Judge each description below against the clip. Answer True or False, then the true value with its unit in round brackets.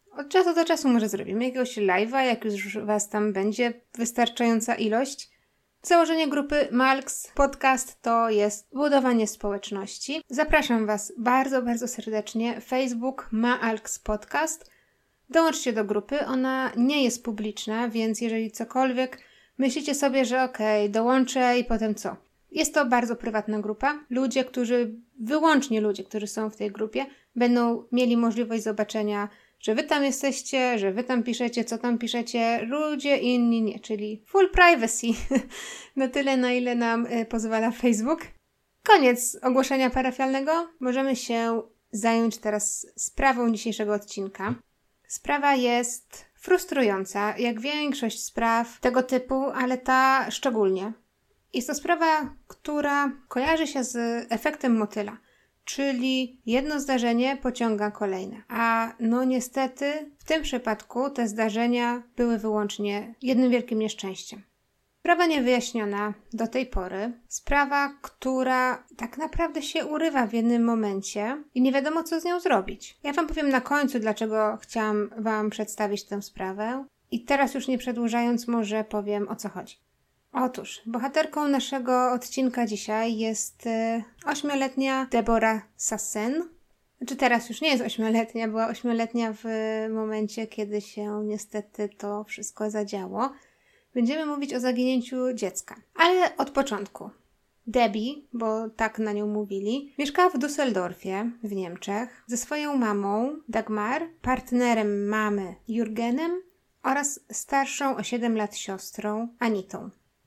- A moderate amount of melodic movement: True (3.5 semitones)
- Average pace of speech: True (130 wpm)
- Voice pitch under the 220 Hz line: False (240 Hz)